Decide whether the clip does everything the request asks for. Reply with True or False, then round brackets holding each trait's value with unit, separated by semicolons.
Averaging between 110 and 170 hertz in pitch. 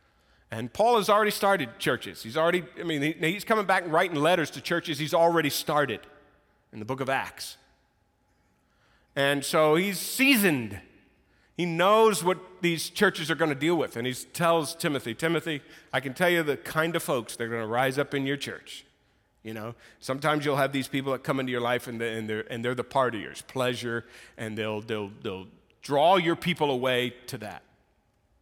True (140 Hz)